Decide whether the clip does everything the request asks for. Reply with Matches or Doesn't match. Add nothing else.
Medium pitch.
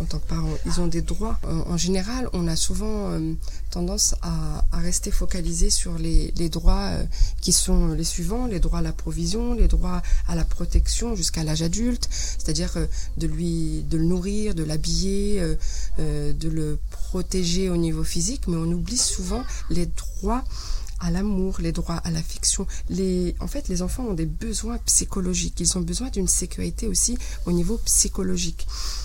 Matches